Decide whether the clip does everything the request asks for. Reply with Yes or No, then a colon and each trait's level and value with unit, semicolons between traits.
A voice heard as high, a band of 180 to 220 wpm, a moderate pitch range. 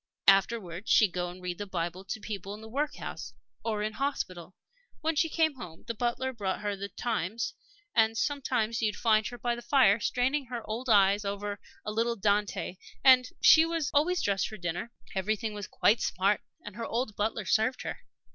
Yes: high, 215 Hz; average, 185 wpm; average, 3.6 semitones